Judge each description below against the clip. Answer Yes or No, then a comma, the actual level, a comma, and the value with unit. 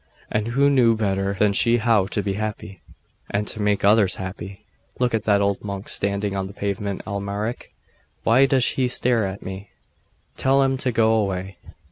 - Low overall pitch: Yes, low, 105 Hz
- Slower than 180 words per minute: No, average, 185 wpm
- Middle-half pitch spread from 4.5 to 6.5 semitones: No, average, 2.8 semitones